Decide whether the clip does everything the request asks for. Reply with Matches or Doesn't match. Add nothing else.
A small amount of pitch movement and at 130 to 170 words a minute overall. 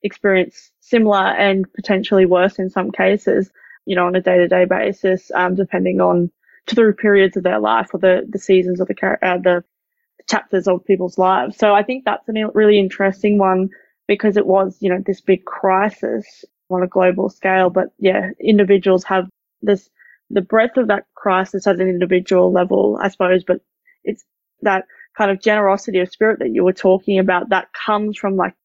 Doesn't match